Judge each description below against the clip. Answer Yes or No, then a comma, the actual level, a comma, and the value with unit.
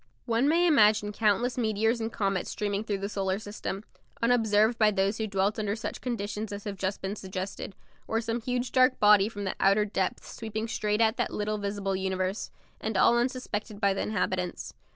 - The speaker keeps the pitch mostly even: Yes, narrow, 2.2 semitones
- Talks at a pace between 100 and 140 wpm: No, average, 190 wpm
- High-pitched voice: Yes, high, 210 Hz